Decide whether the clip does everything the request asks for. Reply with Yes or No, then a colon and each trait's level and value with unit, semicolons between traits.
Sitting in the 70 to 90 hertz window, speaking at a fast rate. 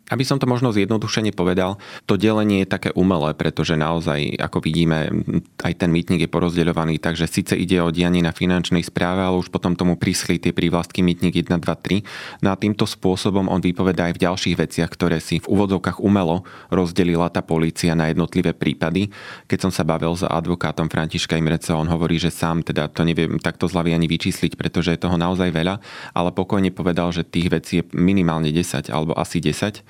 Yes: very low, 85 Hz; fast, 195 wpm